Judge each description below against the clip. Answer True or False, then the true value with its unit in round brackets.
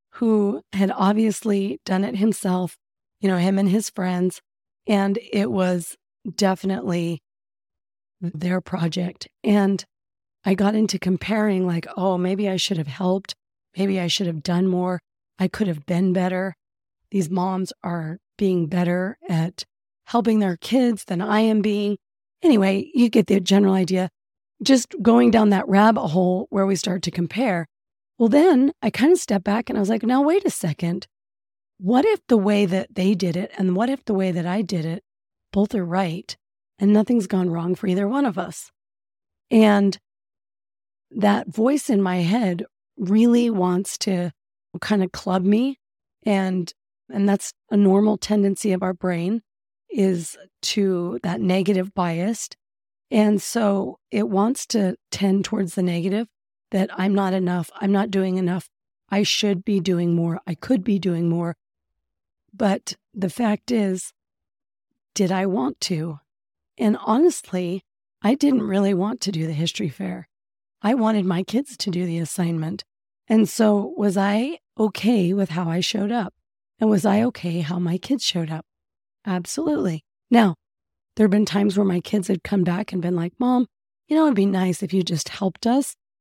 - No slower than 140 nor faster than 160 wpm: False (170 wpm)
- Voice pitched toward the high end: True (195 Hz)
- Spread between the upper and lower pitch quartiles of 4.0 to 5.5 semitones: False (2.9 semitones)